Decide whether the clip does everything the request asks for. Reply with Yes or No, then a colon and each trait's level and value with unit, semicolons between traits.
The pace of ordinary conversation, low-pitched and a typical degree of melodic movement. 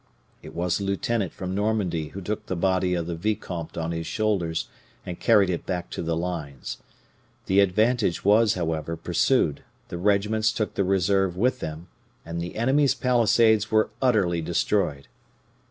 Yes: average, 160 wpm; very low, 95 Hz; average, 4.1 semitones